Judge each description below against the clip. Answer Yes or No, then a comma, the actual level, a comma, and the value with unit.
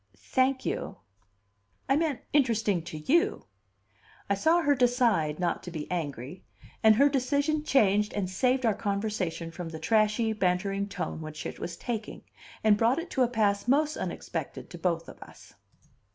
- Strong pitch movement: Yes, wide, 6.4 semitones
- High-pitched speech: Yes, high, 215 Hz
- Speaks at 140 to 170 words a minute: Yes, average, 165 wpm